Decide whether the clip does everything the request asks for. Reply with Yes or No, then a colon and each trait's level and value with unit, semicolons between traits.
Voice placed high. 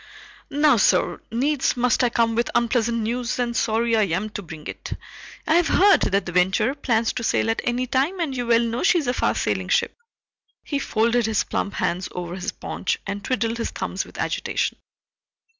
Yes: high, 235 Hz